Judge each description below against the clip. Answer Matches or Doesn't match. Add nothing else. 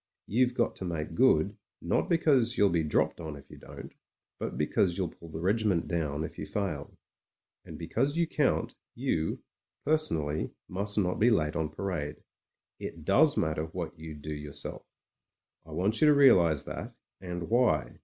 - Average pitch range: Doesn't match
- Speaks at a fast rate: Doesn't match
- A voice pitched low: Matches